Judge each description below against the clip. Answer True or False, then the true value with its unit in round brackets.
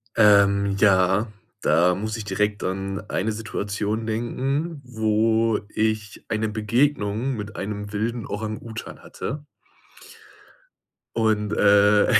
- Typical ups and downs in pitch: False (1.7 semitones)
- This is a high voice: False (105 Hz)